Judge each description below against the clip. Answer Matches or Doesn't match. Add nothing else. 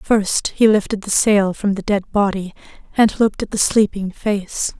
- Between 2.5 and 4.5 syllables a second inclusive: Matches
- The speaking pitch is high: Matches